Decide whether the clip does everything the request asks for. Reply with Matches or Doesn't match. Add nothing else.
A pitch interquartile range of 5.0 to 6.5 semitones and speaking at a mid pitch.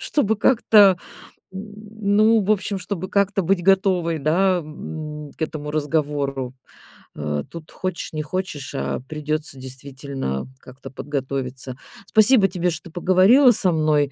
Matches